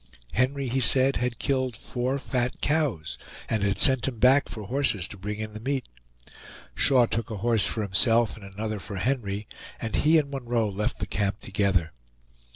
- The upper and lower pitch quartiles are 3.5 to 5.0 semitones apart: Yes, average, 4.2 semitones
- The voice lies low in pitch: Yes, low, 115 Hz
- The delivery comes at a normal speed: Yes, average, 180 wpm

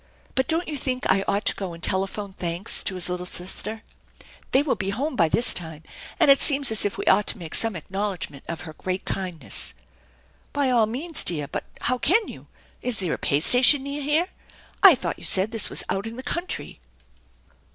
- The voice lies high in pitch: Yes, high, 210 Hz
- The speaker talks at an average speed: No, fast, 215 wpm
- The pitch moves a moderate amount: No, wide, 6.7 semitones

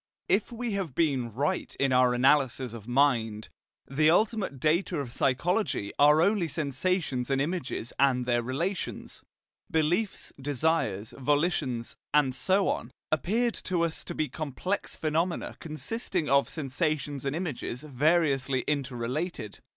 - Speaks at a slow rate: Yes, slow, 130 wpm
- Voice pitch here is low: No, medium, 145 Hz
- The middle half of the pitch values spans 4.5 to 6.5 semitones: Yes, average, 4.9 semitones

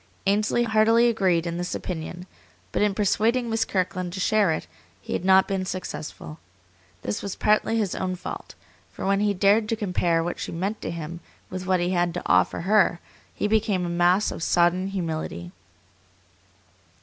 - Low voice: No, medium, 185 Hz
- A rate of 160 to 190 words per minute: Yes, average, 175 wpm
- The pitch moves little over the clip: No, average, 3.2 semitones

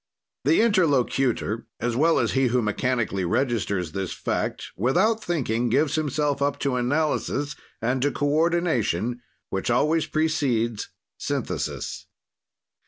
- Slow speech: Yes, slow, 115 wpm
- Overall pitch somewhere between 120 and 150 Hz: Yes, low, 135 Hz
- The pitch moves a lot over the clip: No, average, 4.7 semitones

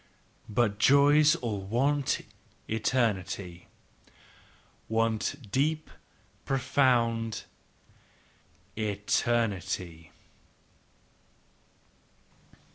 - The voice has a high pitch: No, low, 115 Hz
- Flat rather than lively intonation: No, average, 4.8 semitones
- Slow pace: Yes, slow, 45 wpm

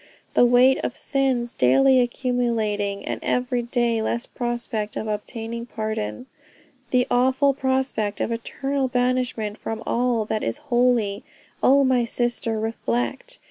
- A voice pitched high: Yes, high, 240 Hz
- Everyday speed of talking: No, slow, 130 wpm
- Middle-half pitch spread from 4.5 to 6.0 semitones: No, narrow, 2.6 semitones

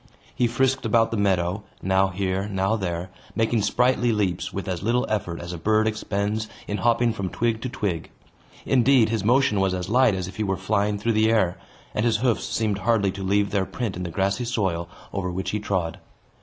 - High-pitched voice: No, low, 105 Hz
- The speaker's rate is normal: No, fast, 210 wpm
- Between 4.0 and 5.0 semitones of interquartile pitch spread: No, average, 3.1 semitones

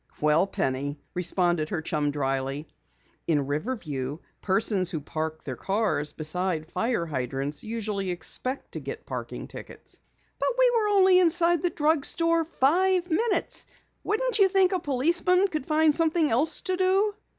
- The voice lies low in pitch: No, high, 230 Hz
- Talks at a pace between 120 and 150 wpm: Yes, average, 145 wpm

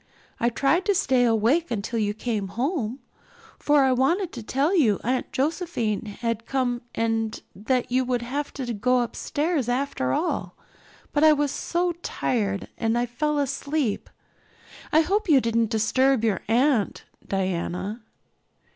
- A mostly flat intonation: No, average, 4.4 semitones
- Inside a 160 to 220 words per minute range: No, average, 145 wpm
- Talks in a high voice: Yes, high, 245 Hz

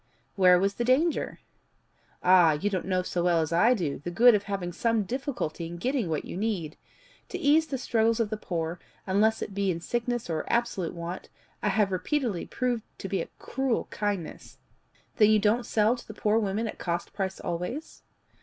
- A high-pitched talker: Yes, high, 205 Hz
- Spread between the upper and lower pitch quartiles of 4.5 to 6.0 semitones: Yes, average, 4.9 semitones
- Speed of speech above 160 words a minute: Yes, average, 195 wpm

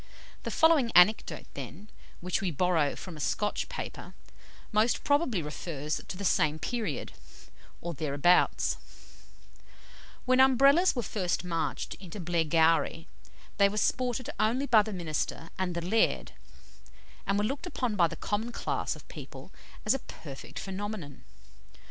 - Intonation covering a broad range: Yes, wide, 5.7 semitones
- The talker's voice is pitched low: No, high, 190 Hz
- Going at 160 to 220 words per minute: No, average, 140 wpm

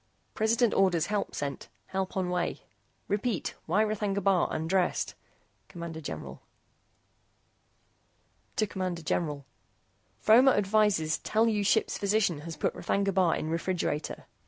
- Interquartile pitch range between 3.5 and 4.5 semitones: Yes, average, 3.9 semitones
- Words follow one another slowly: Yes, slow, 115 wpm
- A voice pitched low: No, high, 190 Hz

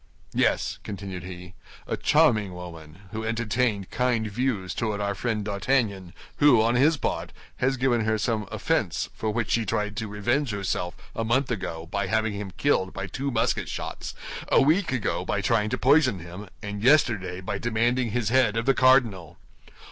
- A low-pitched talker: Yes, low, 110 Hz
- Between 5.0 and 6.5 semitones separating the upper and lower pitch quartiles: No, average, 4.1 semitones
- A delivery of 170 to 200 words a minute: Yes, average, 175 wpm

